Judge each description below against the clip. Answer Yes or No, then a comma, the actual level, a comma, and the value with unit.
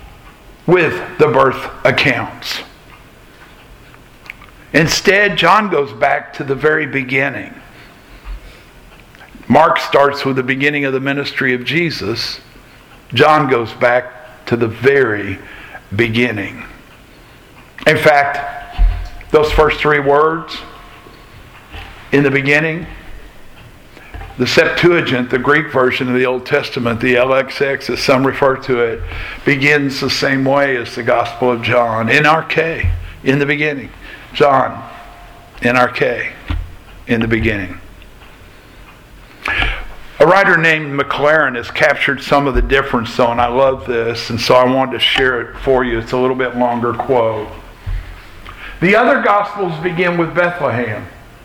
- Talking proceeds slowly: Yes, slow, 130 wpm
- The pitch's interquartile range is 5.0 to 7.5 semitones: No, average, 3.8 semitones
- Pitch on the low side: Yes, low, 130 Hz